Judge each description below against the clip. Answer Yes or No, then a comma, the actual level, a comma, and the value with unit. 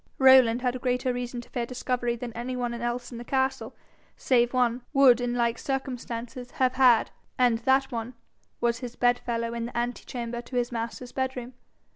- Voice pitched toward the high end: Yes, high, 245 Hz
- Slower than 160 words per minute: No, average, 180 wpm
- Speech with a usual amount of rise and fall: No, narrow, 1.2 semitones